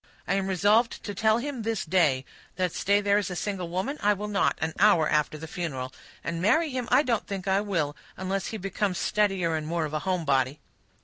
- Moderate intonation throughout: Yes, average, 4.2 semitones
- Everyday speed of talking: No, fast, 215 wpm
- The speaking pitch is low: No, high, 190 Hz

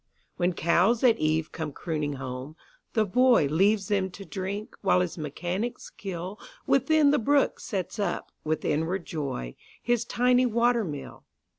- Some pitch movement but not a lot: No, wide, 6.8 semitones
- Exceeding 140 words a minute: No, slow, 135 wpm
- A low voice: No, high, 190 Hz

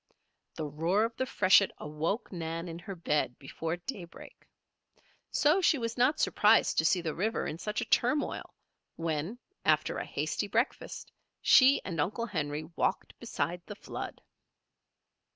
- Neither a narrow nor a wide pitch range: No, wide, 6.1 semitones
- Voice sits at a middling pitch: Yes, medium, 180 Hz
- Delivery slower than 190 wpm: Yes, average, 150 wpm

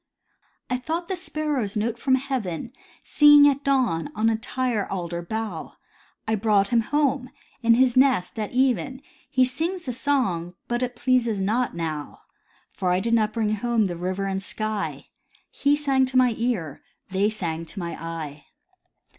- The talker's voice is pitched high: Yes, high, 230 Hz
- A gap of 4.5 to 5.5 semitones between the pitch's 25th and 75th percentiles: Yes, average, 5.2 semitones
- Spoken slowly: No, average, 165 wpm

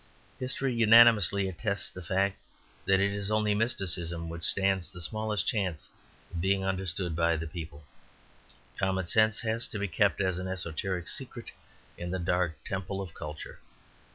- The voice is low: Yes, very low, 95 Hz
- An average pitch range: Yes, average, 3.1 semitones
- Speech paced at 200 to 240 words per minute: No, average, 155 wpm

